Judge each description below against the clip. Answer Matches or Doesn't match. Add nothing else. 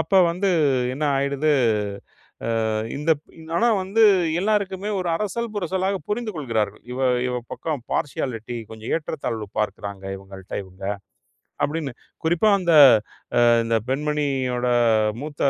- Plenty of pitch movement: Matches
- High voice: Doesn't match